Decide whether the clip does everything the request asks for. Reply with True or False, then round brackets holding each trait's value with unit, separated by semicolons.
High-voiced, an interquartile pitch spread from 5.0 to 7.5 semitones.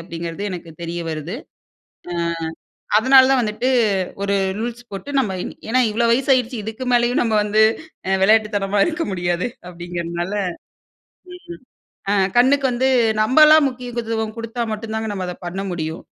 True (220 Hz; 5.3 semitones)